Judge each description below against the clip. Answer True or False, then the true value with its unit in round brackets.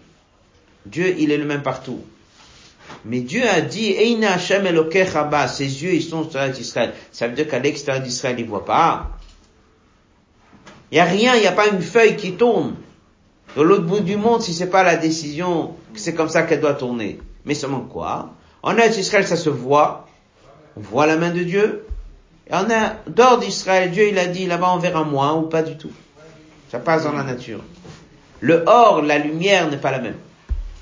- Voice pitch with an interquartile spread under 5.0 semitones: False (5.5 semitones)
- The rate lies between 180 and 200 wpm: True (195 wpm)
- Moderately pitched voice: True (160 Hz)